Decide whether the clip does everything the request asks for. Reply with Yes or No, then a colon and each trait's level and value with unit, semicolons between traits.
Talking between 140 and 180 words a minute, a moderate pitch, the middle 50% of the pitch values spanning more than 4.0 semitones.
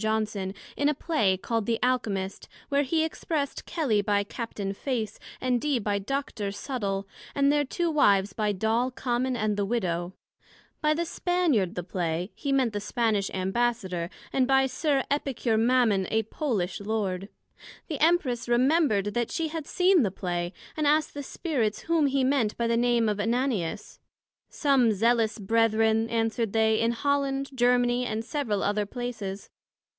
No: average, 160 wpm; high, 230 Hz; average, 5.0 semitones